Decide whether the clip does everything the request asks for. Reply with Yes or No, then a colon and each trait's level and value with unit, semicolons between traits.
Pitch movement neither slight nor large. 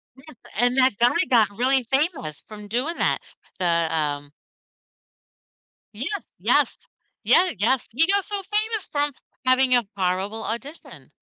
No: wide, 6.3 semitones